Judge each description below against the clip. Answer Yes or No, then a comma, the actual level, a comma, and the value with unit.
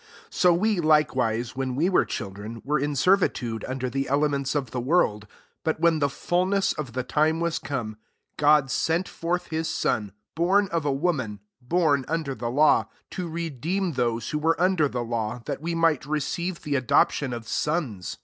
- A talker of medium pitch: Yes, medium, 145 Hz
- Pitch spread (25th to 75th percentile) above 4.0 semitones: Yes, average, 5.1 semitones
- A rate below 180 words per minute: No, average, 190 wpm